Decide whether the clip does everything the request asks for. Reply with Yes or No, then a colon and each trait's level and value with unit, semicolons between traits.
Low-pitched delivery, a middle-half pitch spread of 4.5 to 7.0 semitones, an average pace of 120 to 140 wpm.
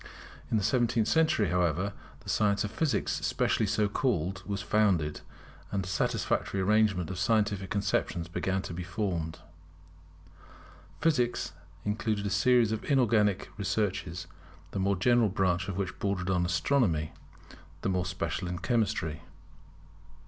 No: low, 100 Hz; average, 3.2 semitones; slow, 135 wpm